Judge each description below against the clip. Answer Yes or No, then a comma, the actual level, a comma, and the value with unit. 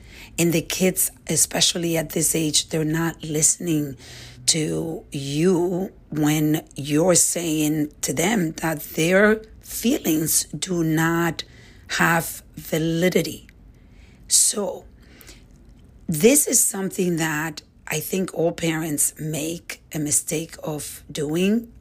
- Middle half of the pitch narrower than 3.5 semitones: Yes, narrow, 2.4 semitones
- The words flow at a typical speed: No, slow, 105 wpm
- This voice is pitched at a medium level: Yes, medium, 160 Hz